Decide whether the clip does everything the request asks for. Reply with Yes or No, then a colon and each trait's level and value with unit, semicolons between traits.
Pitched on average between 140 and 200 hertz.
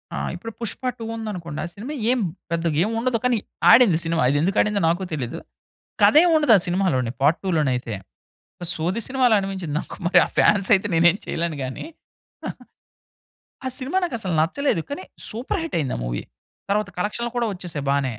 Yes: high, 190 Hz